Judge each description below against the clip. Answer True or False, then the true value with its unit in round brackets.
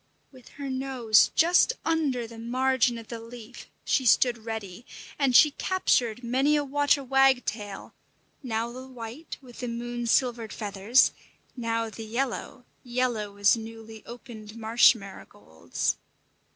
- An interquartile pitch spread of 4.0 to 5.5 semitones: False (2.8 semitones)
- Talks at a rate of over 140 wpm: False (135 wpm)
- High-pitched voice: True (240 Hz)